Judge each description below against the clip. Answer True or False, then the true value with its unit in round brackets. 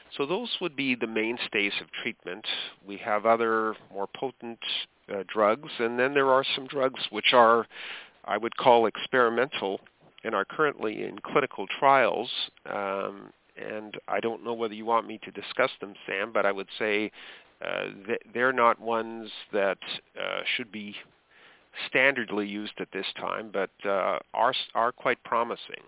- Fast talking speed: False (160 wpm)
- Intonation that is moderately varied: True (3.2 semitones)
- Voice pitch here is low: True (115 Hz)